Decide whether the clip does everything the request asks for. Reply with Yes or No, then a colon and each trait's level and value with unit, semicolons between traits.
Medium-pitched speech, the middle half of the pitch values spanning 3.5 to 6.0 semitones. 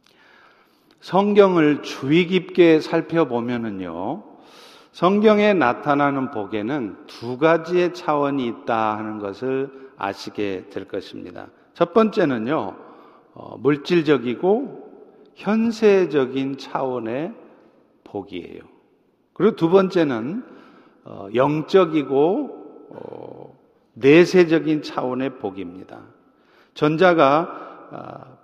No: medium, 160 Hz; wide, 6.8 semitones